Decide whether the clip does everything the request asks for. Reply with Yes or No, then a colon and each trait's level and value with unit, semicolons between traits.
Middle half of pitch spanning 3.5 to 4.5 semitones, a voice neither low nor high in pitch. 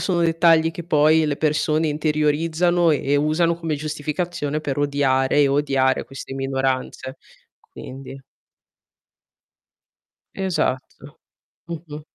No: average, 2.9 semitones; medium, 150 Hz